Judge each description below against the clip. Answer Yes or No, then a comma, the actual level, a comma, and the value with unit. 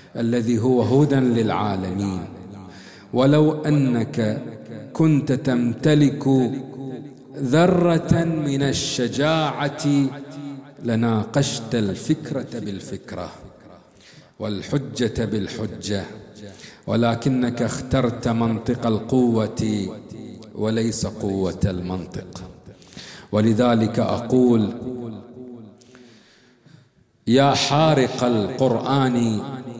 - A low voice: Yes, low, 120 Hz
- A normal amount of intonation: Yes, average, 3.5 semitones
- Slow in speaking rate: Yes, slow, 55 wpm